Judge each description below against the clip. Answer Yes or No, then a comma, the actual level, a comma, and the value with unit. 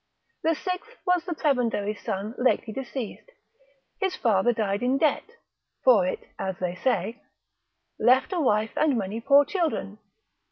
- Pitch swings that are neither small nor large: No, wide, 6.6 semitones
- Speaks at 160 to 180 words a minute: No, average, 145 wpm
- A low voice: No, high, 245 Hz